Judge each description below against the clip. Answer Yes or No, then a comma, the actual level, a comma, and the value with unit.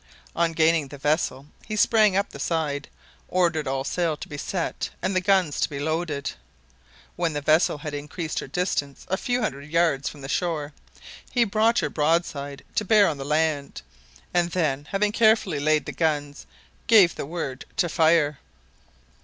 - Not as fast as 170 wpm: No, average, 175 wpm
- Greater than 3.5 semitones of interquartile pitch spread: Yes, average, 3.9 semitones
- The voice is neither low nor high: Yes, medium, 160 Hz